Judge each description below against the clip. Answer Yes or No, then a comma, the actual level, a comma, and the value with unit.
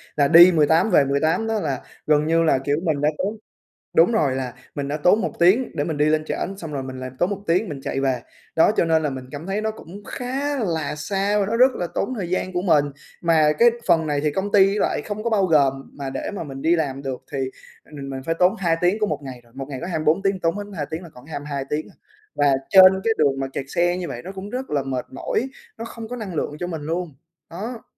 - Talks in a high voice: No, medium, 165 Hz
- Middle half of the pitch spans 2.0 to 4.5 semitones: No, average, 5.3 semitones